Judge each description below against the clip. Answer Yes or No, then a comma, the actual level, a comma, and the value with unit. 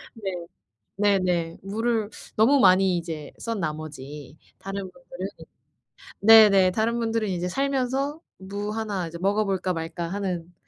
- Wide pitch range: No, average, 4.1 semitones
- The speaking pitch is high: Yes, high, 195 Hz